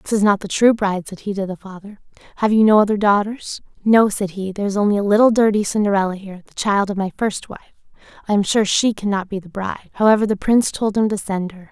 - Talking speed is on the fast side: Yes, fast, 250 wpm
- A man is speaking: No, female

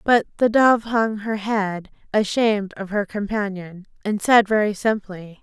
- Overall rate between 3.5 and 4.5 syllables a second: Yes, 4.2 syllables/s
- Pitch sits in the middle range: No, high, 210 Hz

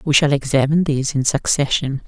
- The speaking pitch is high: No, medium, 140 Hz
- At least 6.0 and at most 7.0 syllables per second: Yes, 6.1 syllables/s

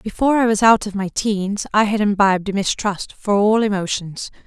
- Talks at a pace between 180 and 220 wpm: Yes, average, 200 wpm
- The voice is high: Yes, high, 205 Hz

